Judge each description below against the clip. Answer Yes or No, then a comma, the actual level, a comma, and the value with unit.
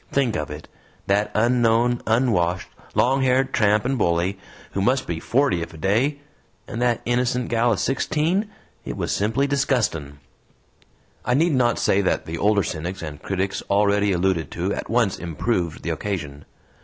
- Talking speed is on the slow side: No, average, 160 wpm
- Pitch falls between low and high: No, low, 105 Hz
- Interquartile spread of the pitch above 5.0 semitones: Yes, wide, 5.4 semitones